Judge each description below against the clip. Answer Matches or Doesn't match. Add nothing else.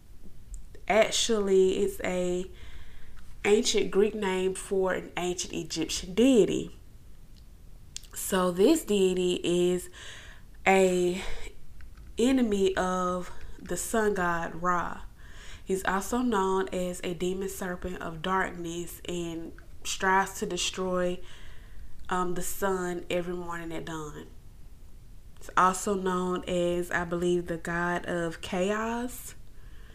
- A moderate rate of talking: Doesn't match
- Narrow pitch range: Matches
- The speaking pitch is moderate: Matches